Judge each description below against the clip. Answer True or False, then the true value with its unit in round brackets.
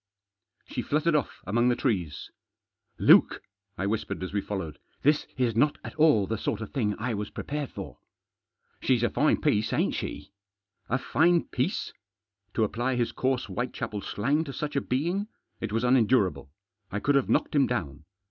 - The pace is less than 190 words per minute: False (195 wpm)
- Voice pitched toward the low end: True (120 Hz)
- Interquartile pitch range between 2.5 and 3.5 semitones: False (5.3 semitones)